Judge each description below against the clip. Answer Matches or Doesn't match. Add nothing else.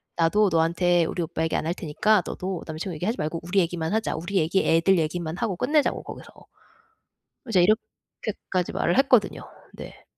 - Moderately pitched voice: Matches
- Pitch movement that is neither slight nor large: Matches